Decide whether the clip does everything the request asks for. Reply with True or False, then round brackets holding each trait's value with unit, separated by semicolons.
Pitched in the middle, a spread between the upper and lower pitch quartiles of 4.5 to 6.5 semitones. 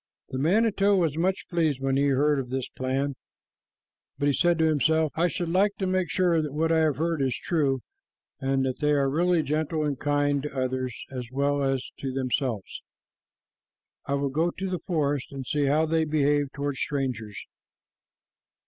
False (145 Hz; 3.3 semitones)